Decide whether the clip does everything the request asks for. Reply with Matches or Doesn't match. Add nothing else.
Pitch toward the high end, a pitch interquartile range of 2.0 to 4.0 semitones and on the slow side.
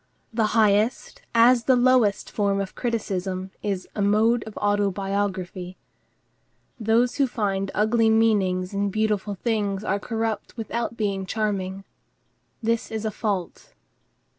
Matches